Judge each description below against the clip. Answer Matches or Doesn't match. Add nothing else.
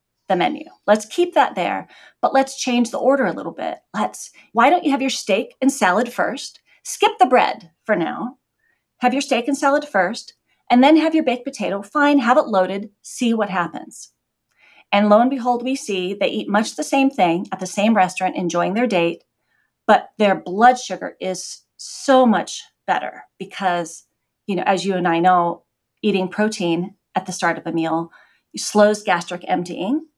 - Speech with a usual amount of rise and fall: Doesn't match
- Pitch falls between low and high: Doesn't match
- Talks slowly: Doesn't match